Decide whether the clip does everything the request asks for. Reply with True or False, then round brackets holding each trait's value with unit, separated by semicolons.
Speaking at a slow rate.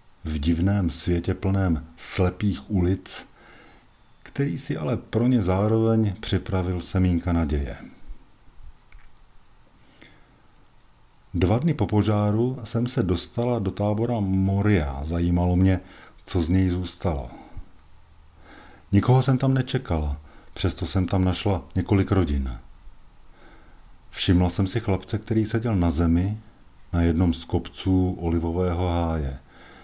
True (110 wpm)